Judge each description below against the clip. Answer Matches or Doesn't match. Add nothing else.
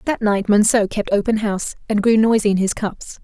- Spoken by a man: Doesn't match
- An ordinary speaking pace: Doesn't match